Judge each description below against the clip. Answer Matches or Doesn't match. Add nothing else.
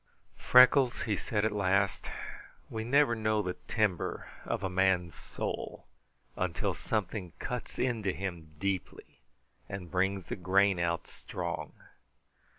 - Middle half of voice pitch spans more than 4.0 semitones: Doesn't match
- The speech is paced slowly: Matches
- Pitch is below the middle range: Matches